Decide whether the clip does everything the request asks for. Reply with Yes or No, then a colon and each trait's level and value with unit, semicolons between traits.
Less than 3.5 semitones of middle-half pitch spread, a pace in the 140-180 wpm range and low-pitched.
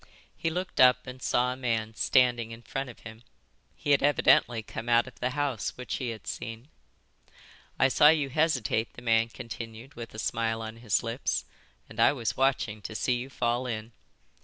No: narrow, 2.5 semitones; average, 190 wpm; low, 120 Hz